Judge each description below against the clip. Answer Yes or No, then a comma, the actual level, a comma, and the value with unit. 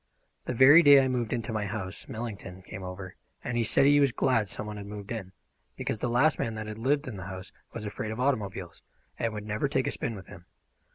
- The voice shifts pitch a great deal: No, average, 4.0 semitones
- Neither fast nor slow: No, fast, 235 wpm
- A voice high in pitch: No, low, 110 Hz